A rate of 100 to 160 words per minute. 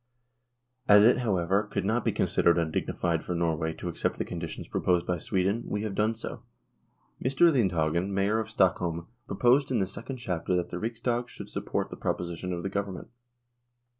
No: average, 175 wpm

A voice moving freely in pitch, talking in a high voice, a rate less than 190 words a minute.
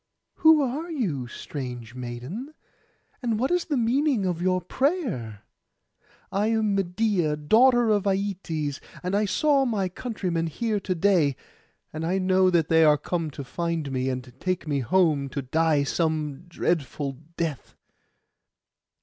No: wide, 6.6 semitones; medium, 175 Hz; average, 145 wpm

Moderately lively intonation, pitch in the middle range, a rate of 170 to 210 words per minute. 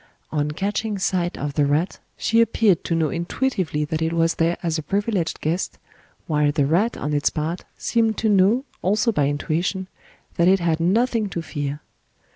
Yes: average, 4.9 semitones; medium, 170 Hz; average, 180 wpm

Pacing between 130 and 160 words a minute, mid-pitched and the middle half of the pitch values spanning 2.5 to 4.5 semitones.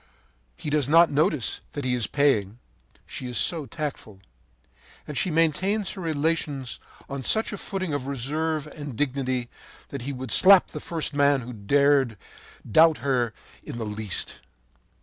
Yes: average, 155 wpm; medium, 145 Hz; average, 4.1 semitones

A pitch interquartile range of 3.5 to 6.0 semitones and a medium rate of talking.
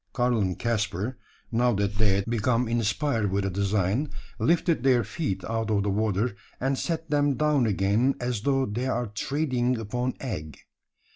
Yes: average, 4.2 semitones; average, 165 wpm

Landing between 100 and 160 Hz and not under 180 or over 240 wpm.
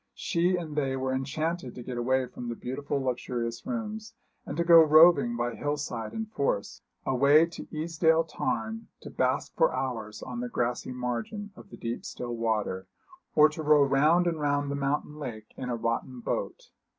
Yes: medium, 140 Hz; average, 185 wpm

